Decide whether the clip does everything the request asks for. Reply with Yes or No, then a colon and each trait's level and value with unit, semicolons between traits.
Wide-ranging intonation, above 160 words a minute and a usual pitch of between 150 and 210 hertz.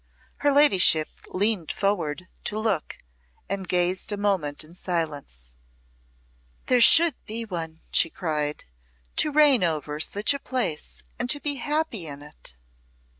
No: wide, 7.4 semitones; slow, 135 wpm; medium, 185 Hz